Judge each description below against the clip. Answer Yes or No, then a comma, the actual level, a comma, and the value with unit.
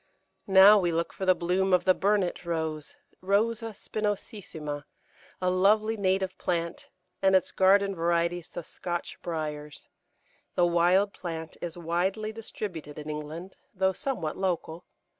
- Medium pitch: Yes, medium, 180 Hz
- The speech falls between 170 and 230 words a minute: No, slow, 135 wpm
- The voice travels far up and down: No, average, 2.8 semitones